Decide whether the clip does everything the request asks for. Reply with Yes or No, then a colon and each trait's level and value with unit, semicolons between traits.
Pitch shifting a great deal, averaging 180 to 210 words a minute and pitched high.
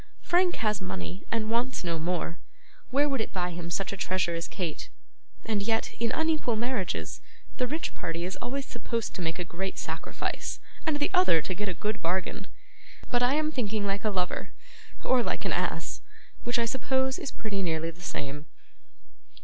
Yes: wide, 5.8 semitones; average, 185 wpm; high, 210 Hz